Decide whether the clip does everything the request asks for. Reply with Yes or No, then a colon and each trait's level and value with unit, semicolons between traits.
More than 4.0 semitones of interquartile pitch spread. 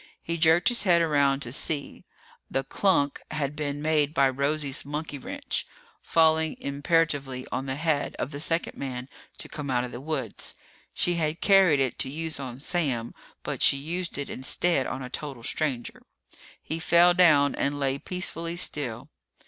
No: average, 3.2 semitones